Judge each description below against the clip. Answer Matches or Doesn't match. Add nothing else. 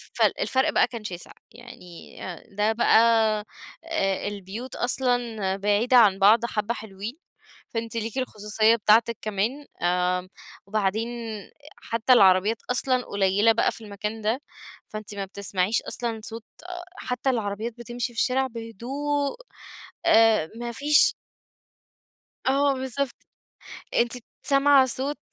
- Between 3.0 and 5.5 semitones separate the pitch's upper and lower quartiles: Matches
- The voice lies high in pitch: Matches